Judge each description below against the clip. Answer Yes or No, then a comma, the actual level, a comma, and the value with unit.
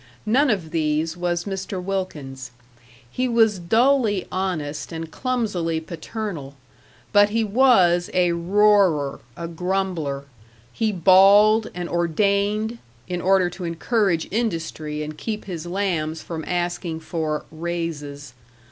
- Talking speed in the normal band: No, slow, 120 wpm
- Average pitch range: Yes, average, 4.1 semitones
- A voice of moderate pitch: Yes, medium, 180 Hz